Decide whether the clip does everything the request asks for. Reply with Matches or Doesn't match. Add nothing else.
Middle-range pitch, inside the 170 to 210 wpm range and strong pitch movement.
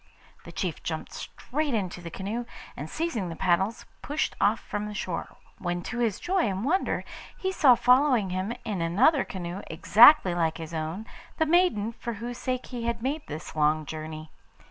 Doesn't match